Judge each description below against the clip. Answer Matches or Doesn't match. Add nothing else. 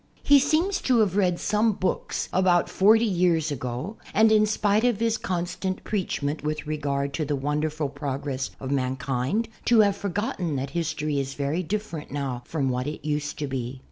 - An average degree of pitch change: Doesn't match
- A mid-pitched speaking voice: Matches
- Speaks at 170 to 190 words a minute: Matches